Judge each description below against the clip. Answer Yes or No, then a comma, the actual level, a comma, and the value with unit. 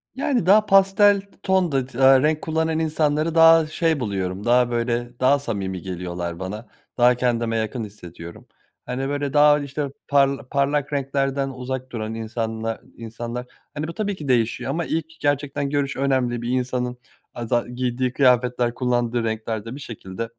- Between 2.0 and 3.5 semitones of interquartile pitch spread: No, average, 3.9 semitones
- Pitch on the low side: Yes, low, 130 Hz